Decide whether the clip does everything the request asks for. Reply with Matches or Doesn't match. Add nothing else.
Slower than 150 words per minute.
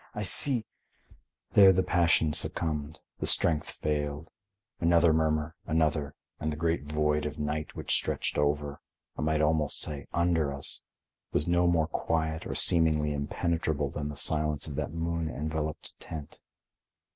Matches